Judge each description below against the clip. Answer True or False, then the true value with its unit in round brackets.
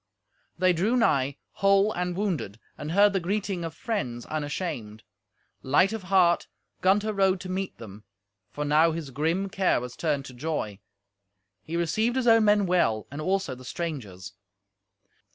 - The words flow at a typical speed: True (155 wpm)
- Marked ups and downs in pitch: True (5.7 semitones)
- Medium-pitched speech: True (170 Hz)